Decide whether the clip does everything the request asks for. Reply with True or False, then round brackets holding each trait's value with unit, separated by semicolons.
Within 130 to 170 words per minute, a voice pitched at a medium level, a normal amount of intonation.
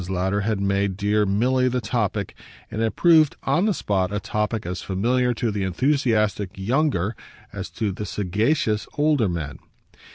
False (160 wpm; 105 Hz; 4.4 semitones)